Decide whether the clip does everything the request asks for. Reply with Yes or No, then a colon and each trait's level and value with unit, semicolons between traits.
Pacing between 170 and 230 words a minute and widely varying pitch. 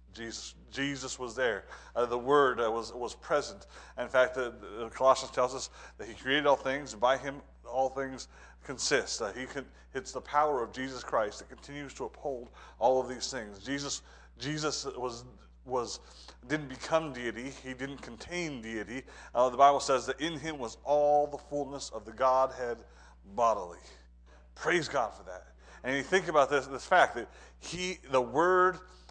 No: average, 185 wpm; average, 3.3 semitones